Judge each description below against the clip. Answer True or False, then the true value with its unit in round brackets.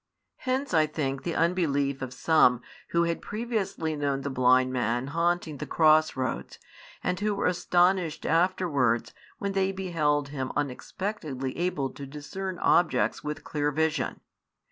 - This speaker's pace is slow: False (145 wpm)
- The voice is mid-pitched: True (155 Hz)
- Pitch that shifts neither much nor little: True (4.8 semitones)